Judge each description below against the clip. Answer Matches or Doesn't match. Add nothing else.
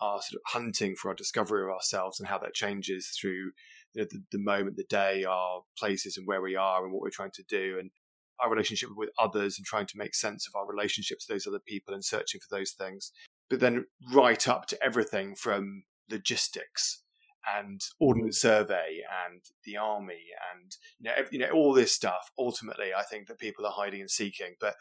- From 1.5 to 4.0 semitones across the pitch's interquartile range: Doesn't match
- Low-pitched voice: Matches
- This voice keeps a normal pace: Doesn't match